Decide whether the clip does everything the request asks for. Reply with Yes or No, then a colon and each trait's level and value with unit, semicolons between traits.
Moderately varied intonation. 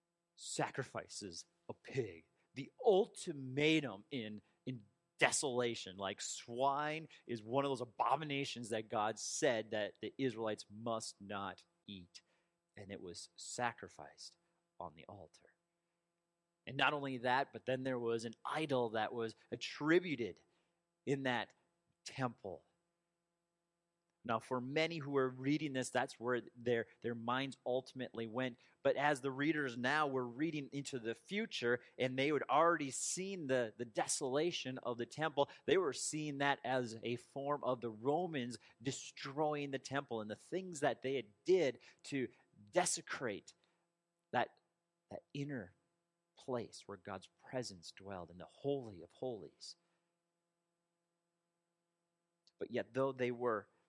No: wide, 6.3 semitones